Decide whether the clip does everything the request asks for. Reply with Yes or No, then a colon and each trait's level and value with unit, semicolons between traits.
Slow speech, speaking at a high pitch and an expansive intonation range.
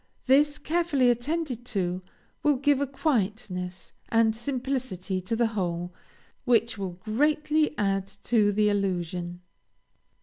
Yes: slow, 115 wpm; high, 225 Hz; wide, 6.6 semitones